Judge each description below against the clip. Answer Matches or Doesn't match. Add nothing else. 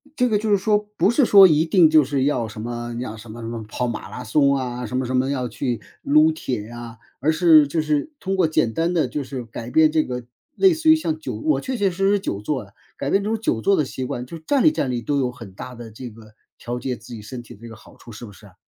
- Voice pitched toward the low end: Matches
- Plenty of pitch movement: Matches